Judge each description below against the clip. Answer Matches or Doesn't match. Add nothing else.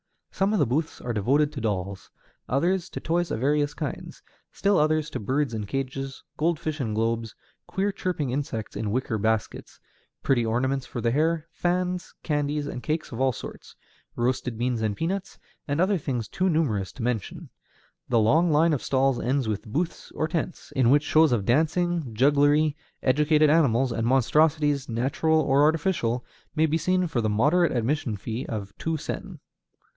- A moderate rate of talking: Matches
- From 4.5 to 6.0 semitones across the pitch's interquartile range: Matches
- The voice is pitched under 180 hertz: Matches